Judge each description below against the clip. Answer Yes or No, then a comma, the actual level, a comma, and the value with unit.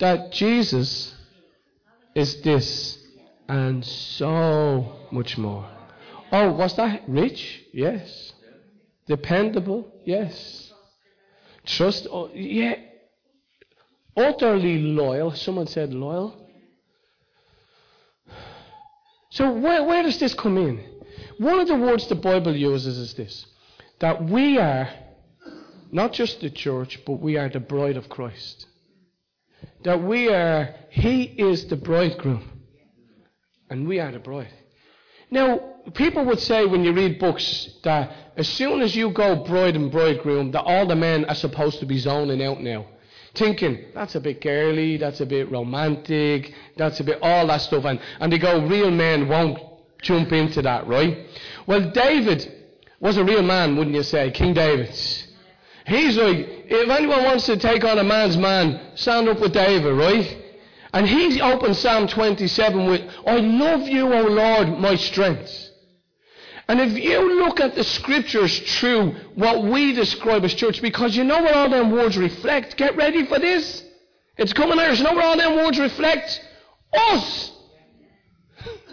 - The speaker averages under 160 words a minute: Yes, average, 150 wpm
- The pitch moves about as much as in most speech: No, wide, 7.6 semitones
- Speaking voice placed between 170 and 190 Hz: Yes, medium, 185 Hz